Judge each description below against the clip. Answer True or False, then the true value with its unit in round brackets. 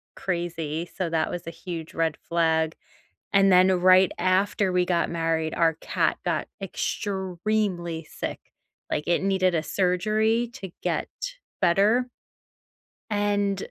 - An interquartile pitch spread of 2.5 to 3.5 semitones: True (2.8 semitones)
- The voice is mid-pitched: True (180 Hz)